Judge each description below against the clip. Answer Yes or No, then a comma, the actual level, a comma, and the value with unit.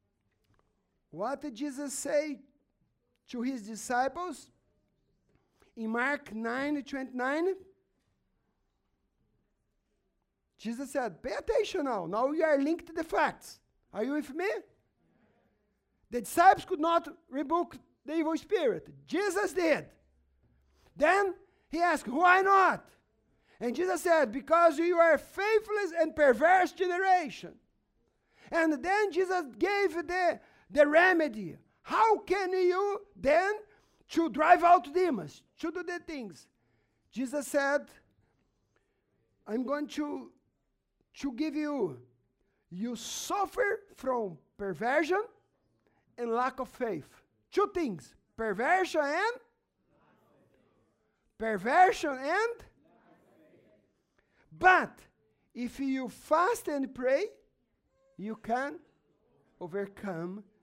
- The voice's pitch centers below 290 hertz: No, very high, 300 Hz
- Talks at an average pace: No, slow, 100 wpm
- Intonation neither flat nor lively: No, wide, 6.8 semitones